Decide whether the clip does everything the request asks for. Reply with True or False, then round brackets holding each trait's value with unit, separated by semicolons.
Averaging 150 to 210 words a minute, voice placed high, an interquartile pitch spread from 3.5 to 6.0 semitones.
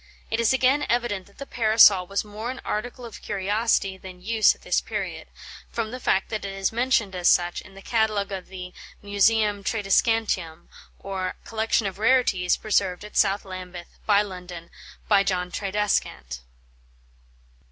False (160 wpm; 200 Hz; 3.1 semitones)